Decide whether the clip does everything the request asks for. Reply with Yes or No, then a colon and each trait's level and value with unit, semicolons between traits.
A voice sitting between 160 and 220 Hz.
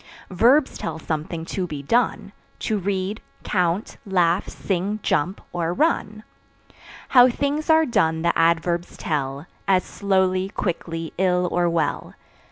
Yes: medium, 185 Hz